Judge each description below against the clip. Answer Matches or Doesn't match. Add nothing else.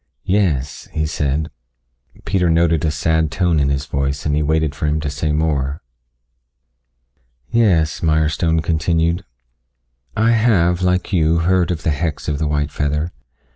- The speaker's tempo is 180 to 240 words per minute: Doesn't match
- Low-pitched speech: Matches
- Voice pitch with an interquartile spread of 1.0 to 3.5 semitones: Matches